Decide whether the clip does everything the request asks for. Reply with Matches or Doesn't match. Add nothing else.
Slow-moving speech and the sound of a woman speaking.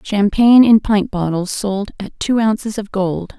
Doesn't match